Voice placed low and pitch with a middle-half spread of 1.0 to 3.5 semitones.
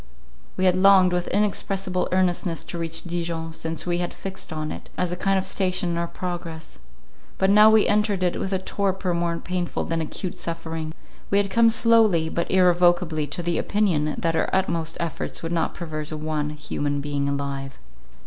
No: medium, 175 Hz; average, 2.7 semitones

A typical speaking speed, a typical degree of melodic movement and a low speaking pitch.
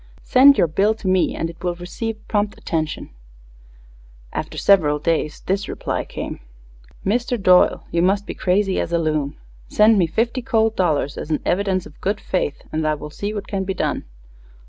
No: average, 185 wpm; average, 4.2 semitones; medium, 185 Hz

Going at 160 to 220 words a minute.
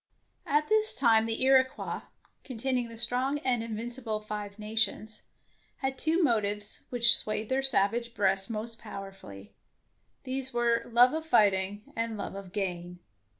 No: average, 145 wpm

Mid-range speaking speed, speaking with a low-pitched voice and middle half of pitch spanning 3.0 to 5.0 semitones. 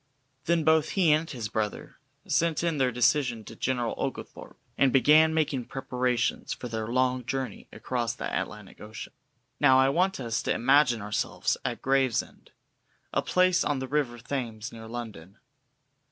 Yes: average, 155 wpm; low, 130 Hz; average, 4.2 semitones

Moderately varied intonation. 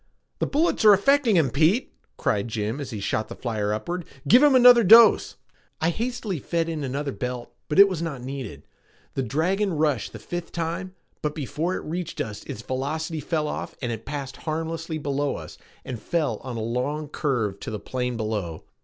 No: wide, 5.9 semitones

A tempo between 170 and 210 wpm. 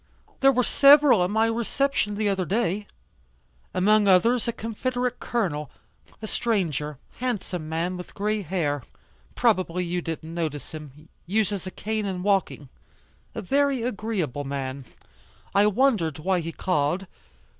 No: slow, 135 wpm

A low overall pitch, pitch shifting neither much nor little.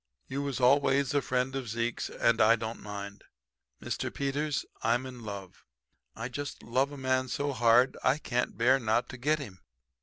Yes: low, 125 Hz; average, 3.0 semitones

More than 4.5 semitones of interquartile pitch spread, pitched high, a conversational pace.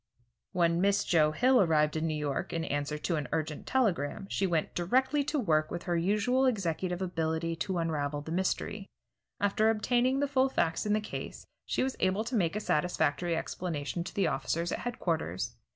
No: average, 5.0 semitones; medium, 175 Hz; average, 185 wpm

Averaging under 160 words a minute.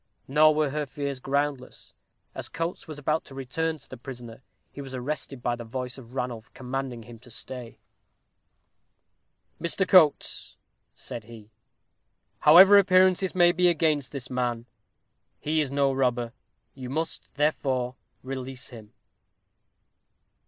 Yes: slow, 135 wpm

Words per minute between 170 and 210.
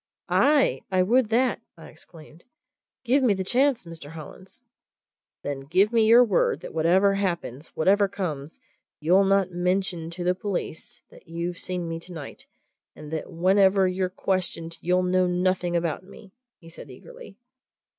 No: average, 155 wpm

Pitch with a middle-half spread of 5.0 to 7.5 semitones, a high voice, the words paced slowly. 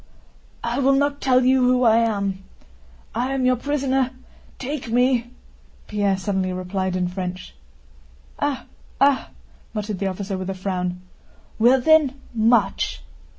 Yes: wide, 5.4 semitones; high, 235 Hz; slow, 130 wpm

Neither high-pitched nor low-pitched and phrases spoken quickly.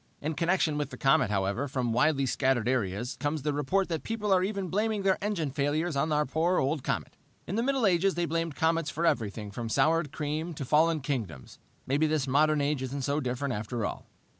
Yes: medium, 150 Hz; fast, 210 wpm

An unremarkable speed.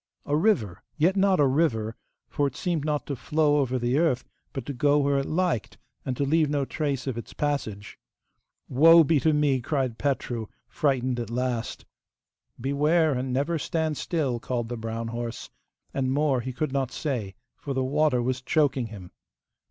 Yes: average, 180 wpm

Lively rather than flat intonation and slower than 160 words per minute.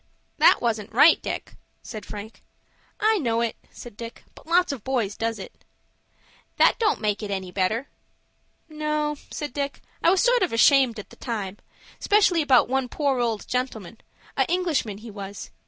No: wide, 6.0 semitones; average, 165 wpm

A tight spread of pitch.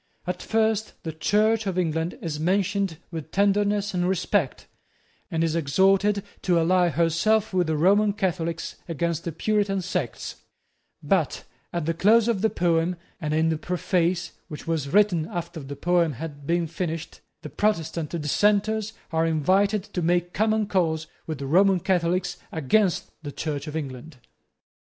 No: average, 3.7 semitones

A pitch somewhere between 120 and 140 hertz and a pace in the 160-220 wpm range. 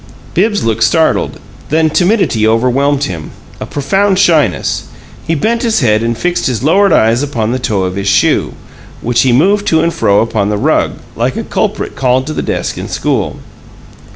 Yes: low, 135 Hz; average, 180 wpm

